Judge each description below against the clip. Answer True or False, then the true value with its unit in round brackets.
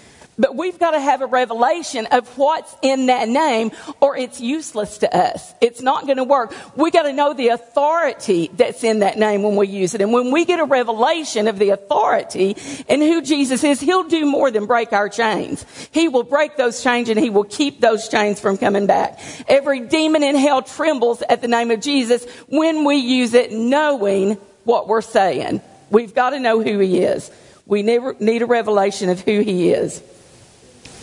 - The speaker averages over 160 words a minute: True (200 wpm)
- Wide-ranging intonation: False (4.7 semitones)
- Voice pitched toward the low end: False (245 Hz)